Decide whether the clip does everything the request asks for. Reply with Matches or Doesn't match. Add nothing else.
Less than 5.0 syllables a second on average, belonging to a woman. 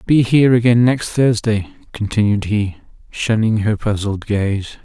Doesn't match